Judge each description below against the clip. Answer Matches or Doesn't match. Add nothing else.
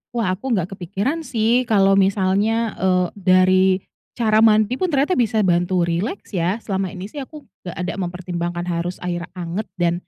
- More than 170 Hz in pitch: Matches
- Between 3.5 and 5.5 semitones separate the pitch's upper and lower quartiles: Matches